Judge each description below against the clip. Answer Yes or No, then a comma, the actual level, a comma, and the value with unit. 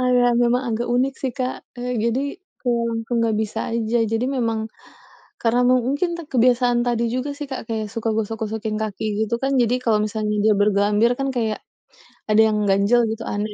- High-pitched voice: Yes, high, 230 Hz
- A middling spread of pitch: No, narrow, 2.2 semitones